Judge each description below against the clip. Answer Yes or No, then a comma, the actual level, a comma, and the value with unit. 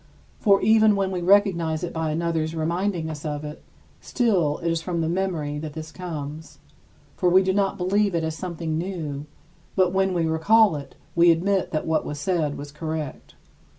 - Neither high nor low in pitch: Yes, medium, 170 Hz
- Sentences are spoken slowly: No, average, 185 wpm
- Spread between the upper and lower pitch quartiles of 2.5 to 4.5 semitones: Yes, average, 3.3 semitones